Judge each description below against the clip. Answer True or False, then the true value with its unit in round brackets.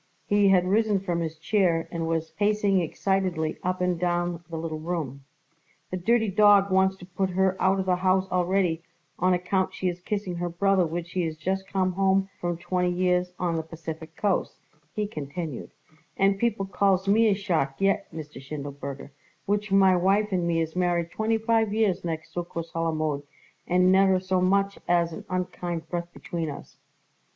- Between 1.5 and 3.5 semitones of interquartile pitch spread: True (2.6 semitones)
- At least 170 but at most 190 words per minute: True (180 wpm)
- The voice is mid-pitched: True (180 Hz)